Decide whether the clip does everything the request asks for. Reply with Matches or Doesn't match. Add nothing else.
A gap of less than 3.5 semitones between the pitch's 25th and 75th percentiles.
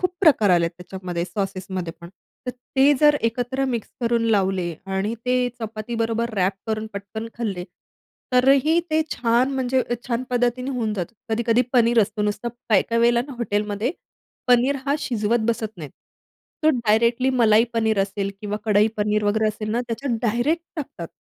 Matches